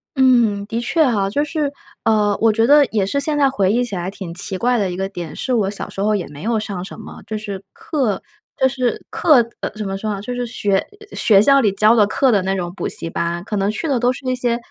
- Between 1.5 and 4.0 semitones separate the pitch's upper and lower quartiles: No, average, 4.5 semitones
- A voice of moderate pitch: No, high, 215 Hz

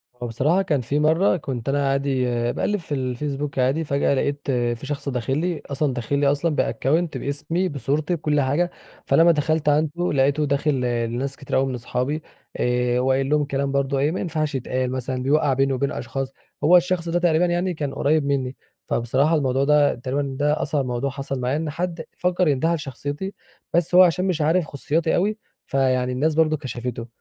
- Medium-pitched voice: Yes, medium, 145 Hz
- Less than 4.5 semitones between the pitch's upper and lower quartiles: Yes, average, 3.2 semitones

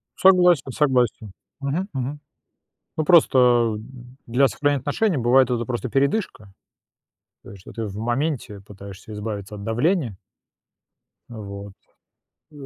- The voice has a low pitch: Yes, low, 125 Hz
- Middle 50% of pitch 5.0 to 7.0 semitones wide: Yes, wide, 5.4 semitones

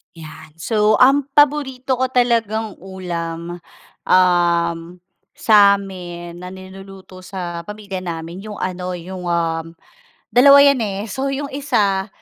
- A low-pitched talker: No, high, 190 Hz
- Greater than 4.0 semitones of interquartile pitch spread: Yes, average, 4.5 semitones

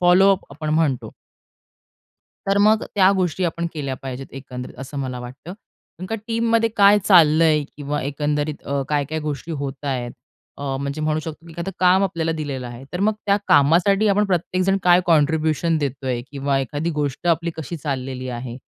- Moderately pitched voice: Yes, medium, 155 Hz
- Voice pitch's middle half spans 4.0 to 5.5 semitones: Yes, average, 4.4 semitones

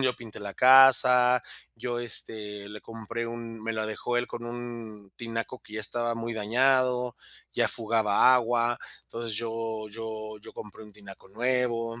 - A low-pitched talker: Yes, low, 115 Hz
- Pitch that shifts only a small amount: Yes, narrow, 2.0 semitones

